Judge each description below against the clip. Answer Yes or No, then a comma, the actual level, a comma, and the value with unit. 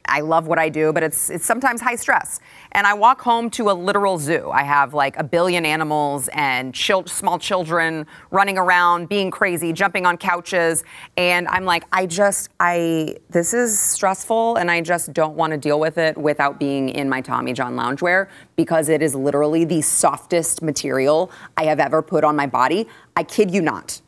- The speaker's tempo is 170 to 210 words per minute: Yes, average, 195 wpm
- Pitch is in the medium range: Yes, medium, 170 Hz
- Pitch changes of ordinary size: Yes, average, 3.5 semitones